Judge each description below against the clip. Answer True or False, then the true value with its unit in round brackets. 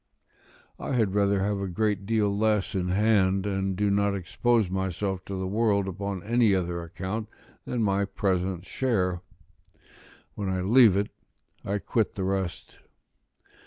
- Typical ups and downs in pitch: False (1.9 semitones)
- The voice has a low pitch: True (100 Hz)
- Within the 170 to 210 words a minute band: False (150 wpm)